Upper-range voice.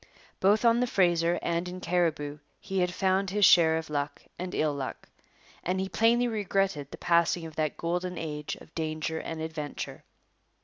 No: medium, 170 Hz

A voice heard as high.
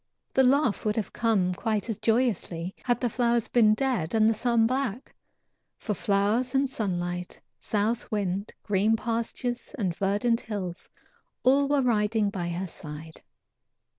Yes: high, 220 Hz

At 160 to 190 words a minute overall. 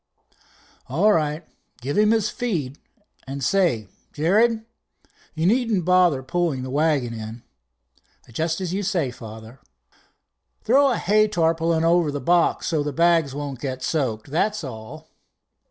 No: average, 140 wpm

